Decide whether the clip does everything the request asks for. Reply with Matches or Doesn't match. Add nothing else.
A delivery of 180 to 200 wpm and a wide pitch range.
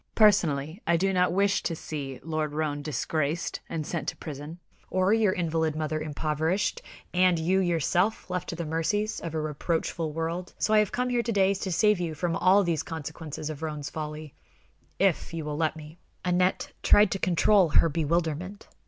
Doesn't match